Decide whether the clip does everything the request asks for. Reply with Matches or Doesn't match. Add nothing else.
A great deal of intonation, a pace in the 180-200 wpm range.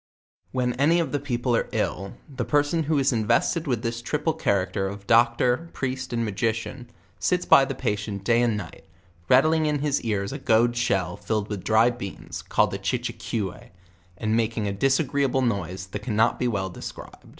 Doesn't match